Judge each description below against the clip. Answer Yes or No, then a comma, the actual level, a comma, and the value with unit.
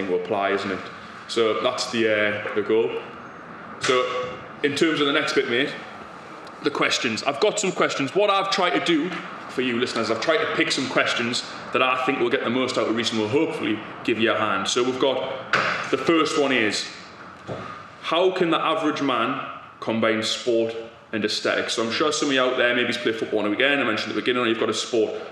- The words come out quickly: Yes, fast, 225 wpm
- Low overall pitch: Yes, low, 125 Hz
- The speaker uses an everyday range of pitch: No, wide, 6.1 semitones